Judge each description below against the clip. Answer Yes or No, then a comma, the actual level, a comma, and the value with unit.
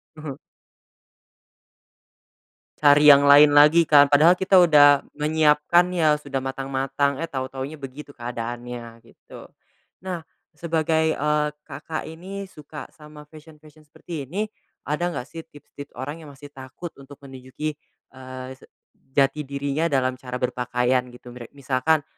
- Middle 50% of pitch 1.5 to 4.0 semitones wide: Yes, average, 2.8 semitones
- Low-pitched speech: No, medium, 145 Hz